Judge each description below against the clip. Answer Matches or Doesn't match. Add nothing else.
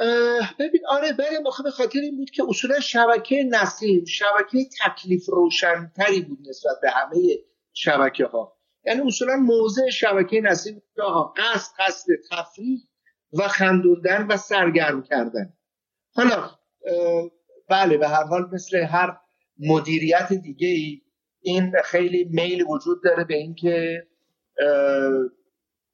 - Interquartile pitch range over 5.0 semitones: Matches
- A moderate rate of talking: Matches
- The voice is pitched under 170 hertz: Doesn't match